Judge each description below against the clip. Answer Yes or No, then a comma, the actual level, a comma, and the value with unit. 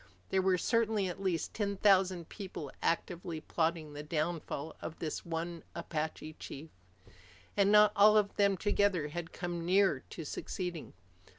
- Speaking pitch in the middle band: Yes, medium, 175 Hz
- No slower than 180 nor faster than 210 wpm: No, average, 150 wpm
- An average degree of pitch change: Yes, average, 3.5 semitones